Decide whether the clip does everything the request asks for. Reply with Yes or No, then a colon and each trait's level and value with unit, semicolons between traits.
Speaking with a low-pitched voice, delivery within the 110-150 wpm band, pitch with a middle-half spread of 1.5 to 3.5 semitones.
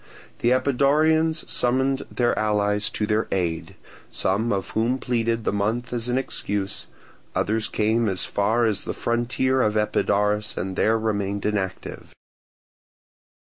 Yes: low, 110 Hz; slow, 135 wpm; average, 3.1 semitones